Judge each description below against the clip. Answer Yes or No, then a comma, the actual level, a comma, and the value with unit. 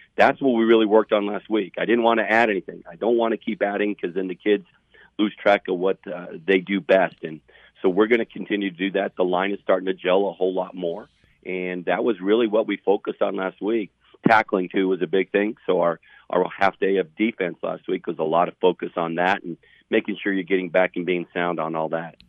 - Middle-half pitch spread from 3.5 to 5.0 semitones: No, narrow, 2.4 semitones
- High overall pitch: No, very low, 95 Hz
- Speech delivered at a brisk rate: Yes, fast, 255 wpm